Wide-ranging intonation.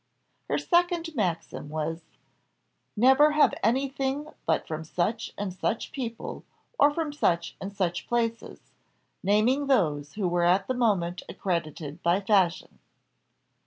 Yes: wide, 7.5 semitones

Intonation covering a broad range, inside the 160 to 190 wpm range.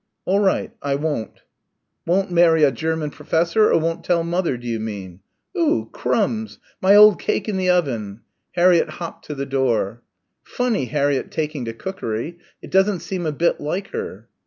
Yes: wide, 5.7 semitones; average, 170 wpm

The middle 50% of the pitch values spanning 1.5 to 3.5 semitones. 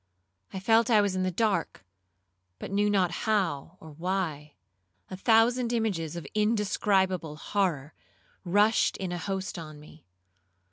No: average, 4.2 semitones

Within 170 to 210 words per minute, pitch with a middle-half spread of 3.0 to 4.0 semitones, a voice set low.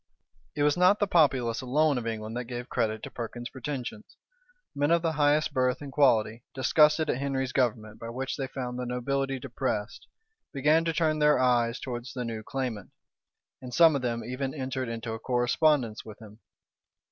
Yes: average, 180 wpm; average, 3.5 semitones; low, 130 Hz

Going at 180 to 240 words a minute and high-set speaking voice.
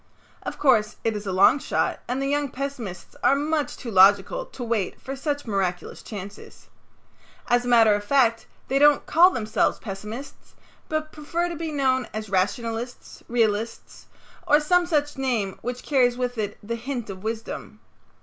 No: average, 170 wpm; high, 245 Hz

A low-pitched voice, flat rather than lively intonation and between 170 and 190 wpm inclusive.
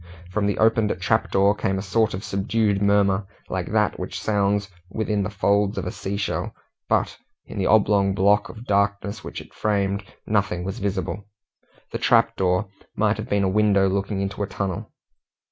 Yes: low, 100 Hz; narrow, 1.2 semitones; average, 180 wpm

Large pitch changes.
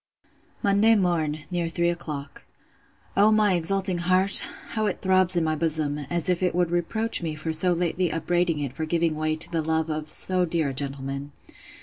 No: average, 2.8 semitones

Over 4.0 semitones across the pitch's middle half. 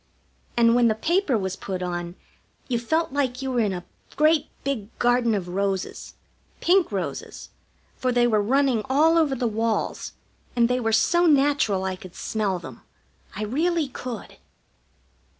Yes: wide, 5.6 semitones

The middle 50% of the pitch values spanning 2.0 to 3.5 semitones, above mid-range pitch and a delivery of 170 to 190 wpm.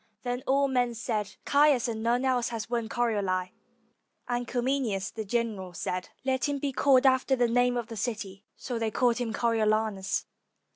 Yes: average, 2.8 semitones; high, 235 Hz; average, 175 wpm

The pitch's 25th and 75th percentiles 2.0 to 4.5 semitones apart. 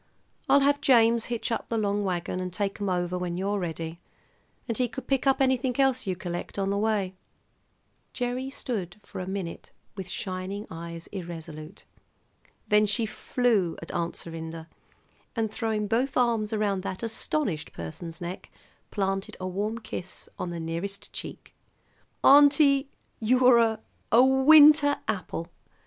No: wide, 5.4 semitones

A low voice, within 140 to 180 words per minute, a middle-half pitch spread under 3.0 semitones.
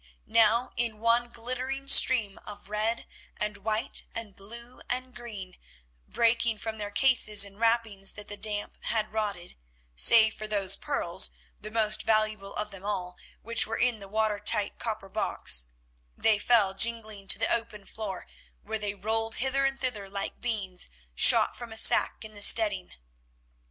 No: high, 215 Hz; average, 155 wpm; narrow, 2.4 semitones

